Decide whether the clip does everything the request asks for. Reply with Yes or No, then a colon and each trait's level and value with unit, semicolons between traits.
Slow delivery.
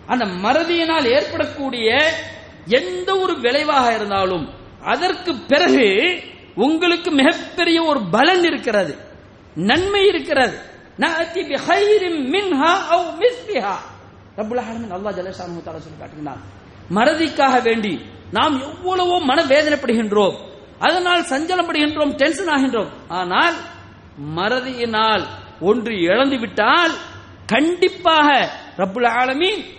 Yes: slow, 95 wpm